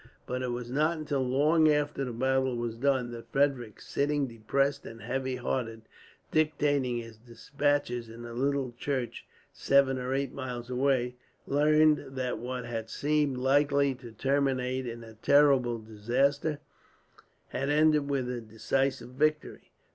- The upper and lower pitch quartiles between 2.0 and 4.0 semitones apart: Yes, average, 2.8 semitones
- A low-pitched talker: Yes, low, 130 Hz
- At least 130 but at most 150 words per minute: Yes, average, 145 wpm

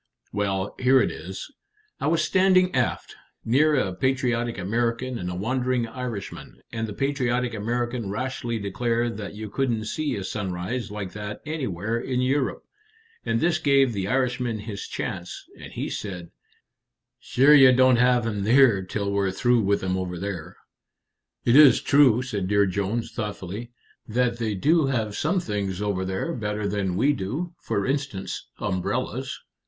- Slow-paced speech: No, average, 155 wpm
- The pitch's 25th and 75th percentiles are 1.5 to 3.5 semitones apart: No, average, 4.4 semitones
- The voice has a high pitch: No, low, 115 Hz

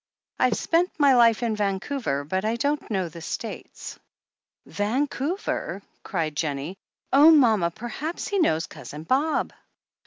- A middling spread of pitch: No, wide, 8.6 semitones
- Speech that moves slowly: Yes, slow, 130 wpm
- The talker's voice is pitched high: Yes, high, 225 Hz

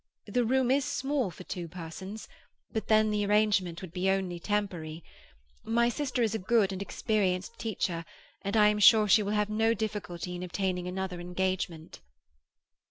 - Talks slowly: No, average, 165 wpm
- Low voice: No, high, 200 Hz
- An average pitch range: Yes, average, 3.3 semitones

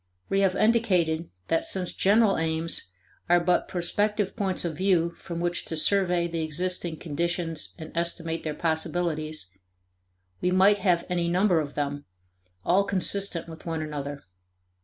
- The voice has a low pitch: No, medium, 170 Hz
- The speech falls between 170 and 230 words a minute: No, average, 145 wpm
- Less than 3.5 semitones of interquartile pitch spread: Yes, average, 2.7 semitones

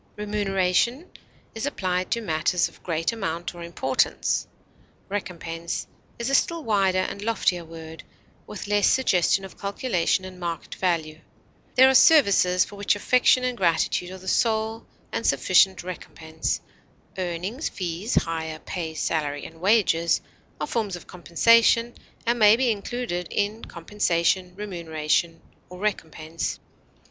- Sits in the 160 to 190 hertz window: Yes, medium, 185 Hz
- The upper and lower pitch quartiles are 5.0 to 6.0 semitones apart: No, average, 4.4 semitones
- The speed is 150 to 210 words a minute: No, slow, 135 wpm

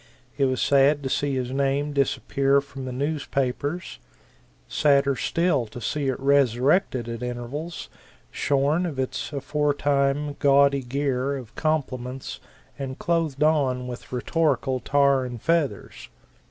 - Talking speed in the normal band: No, slow, 125 wpm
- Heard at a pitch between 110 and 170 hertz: Yes, medium, 140 Hz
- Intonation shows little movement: Yes, narrow, 2.0 semitones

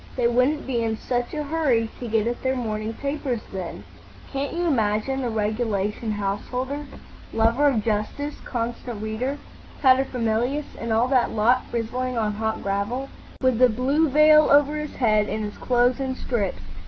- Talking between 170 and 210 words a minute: No, average, 155 wpm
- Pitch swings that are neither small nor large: Yes, average, 3.6 semitones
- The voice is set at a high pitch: Yes, high, 245 Hz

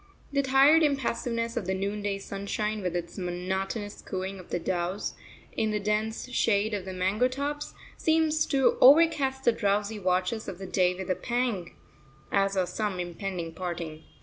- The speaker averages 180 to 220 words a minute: No, average, 160 wpm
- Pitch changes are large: No, average, 4.6 semitones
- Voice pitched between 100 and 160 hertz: No, high, 200 Hz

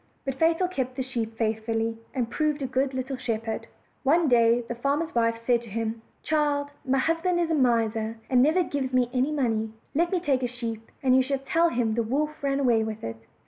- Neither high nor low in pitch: No, very high, 255 Hz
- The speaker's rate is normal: No, fast, 215 wpm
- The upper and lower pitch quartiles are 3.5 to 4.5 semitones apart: Yes, average, 3.9 semitones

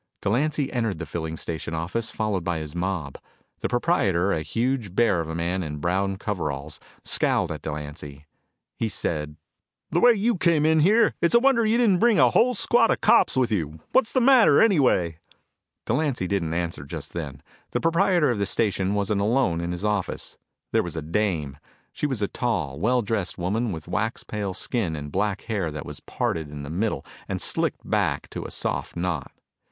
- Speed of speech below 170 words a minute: No, average, 190 wpm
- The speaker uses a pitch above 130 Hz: No, low, 100 Hz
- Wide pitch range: Yes, wide, 7.8 semitones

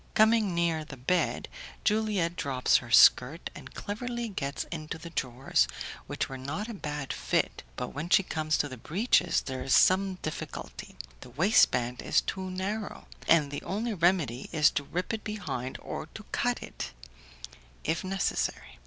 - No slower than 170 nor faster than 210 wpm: No, average, 160 wpm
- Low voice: No, medium, 165 Hz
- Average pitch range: No, wide, 6.0 semitones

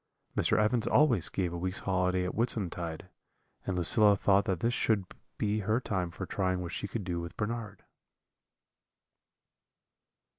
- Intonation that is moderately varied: Yes, average, 3.0 semitones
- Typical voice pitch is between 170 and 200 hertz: No, very low, 95 Hz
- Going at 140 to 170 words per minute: Yes, average, 150 wpm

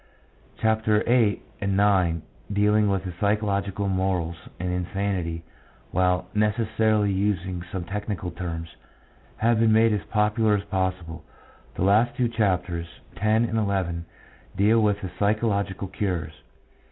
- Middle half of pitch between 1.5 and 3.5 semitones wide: Yes, average, 2.7 semitones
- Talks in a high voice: No, low, 100 Hz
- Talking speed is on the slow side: Yes, slow, 125 wpm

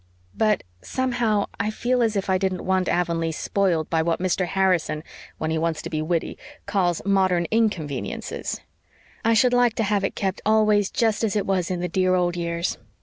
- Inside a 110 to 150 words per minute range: No, average, 190 wpm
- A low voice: No, high, 190 Hz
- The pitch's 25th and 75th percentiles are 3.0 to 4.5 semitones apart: Yes, average, 3.7 semitones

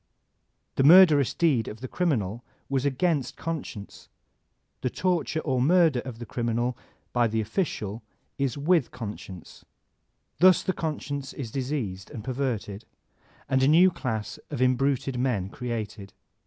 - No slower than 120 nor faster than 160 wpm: Yes, average, 140 wpm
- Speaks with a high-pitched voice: No, low, 130 Hz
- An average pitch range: Yes, average, 4.7 semitones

